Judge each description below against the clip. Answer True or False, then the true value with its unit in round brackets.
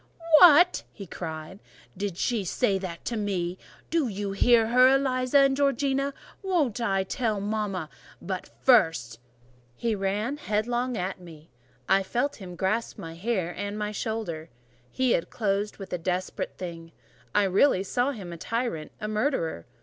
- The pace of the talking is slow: False (155 wpm)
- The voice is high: True (205 Hz)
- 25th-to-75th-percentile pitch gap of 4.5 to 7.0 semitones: True (5.0 semitones)